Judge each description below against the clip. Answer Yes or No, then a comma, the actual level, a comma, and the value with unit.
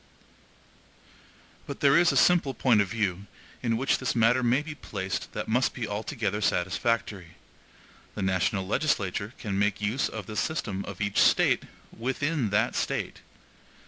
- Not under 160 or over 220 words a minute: No, average, 150 wpm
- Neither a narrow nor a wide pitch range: Yes, average, 4.4 semitones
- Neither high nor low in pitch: No, low, 110 Hz